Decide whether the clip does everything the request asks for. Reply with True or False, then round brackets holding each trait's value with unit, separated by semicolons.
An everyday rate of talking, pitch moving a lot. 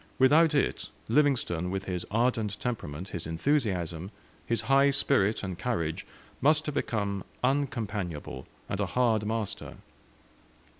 False (120 wpm; 6.3 semitones)